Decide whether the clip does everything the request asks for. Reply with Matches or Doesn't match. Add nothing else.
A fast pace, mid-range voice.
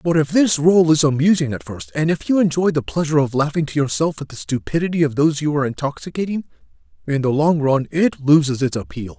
Matches